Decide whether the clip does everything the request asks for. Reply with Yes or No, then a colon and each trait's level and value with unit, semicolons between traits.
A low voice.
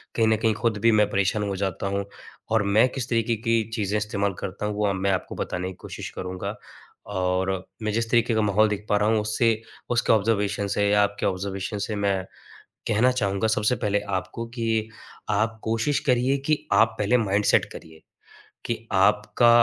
Yes: low, 105 Hz